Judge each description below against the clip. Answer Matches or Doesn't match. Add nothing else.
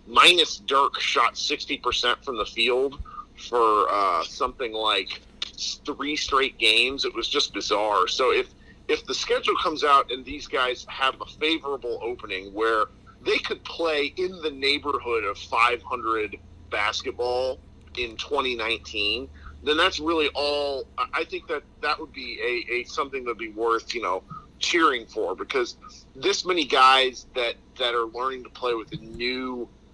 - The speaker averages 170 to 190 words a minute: Doesn't match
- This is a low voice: Doesn't match